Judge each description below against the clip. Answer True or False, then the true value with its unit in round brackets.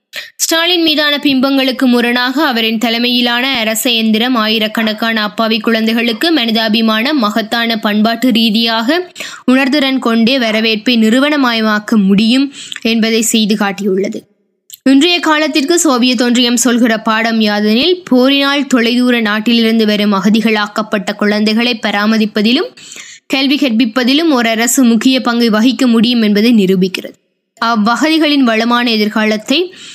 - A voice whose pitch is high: True (235 Hz)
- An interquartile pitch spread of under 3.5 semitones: True (3.0 semitones)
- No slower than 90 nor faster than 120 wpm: True (100 wpm)